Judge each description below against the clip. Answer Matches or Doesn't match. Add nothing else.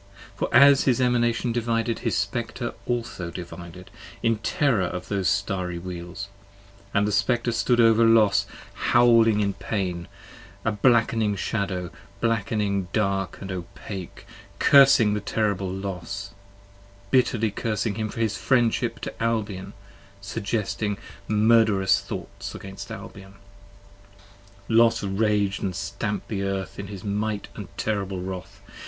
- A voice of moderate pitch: Doesn't match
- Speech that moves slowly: Matches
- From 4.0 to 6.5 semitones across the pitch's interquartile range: Doesn't match